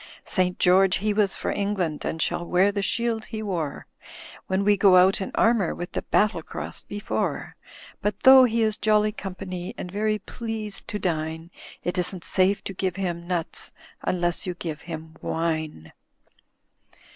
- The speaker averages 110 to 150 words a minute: No, average, 165 wpm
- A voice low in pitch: No, high, 190 Hz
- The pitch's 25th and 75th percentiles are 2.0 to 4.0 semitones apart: Yes, average, 3.2 semitones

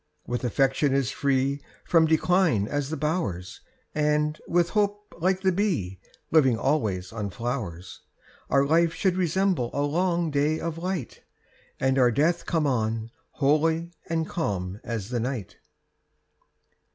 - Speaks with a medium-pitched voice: Yes, medium, 145 Hz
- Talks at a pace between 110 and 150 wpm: Yes, average, 140 wpm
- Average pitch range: No, wide, 5.7 semitones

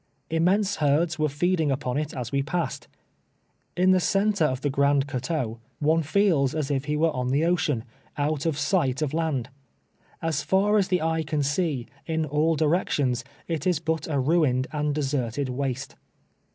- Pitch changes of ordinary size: Yes, average, 3.1 semitones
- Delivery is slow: No, average, 175 wpm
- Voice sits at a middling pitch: Yes, medium, 150 Hz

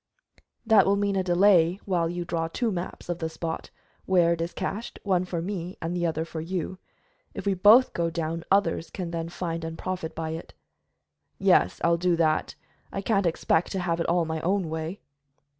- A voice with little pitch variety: Yes, narrow, 2.3 semitones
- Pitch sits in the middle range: Yes, medium, 175 Hz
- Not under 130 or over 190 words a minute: No, average, 200 wpm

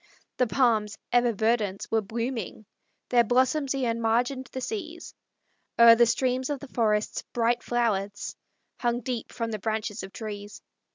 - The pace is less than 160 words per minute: Yes, average, 150 wpm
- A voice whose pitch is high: Yes, high, 235 Hz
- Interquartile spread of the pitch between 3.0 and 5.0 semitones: No, narrow, 2.6 semitones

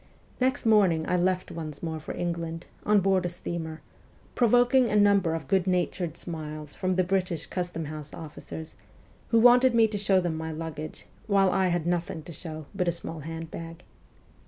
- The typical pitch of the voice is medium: Yes, medium, 175 Hz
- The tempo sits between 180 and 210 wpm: Yes, average, 185 wpm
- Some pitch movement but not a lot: Yes, average, 3.2 semitones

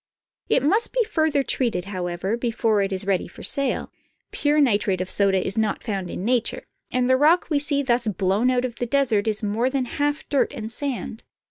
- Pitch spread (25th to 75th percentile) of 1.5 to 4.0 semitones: No, wide, 5.6 semitones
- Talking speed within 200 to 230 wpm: Yes, fast, 205 wpm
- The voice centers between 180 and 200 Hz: No, high, 235 Hz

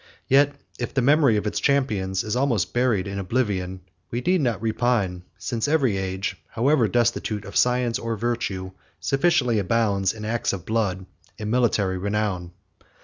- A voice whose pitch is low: Yes, low, 110 Hz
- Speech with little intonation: No, average, 4.2 semitones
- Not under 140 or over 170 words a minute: Yes, average, 155 wpm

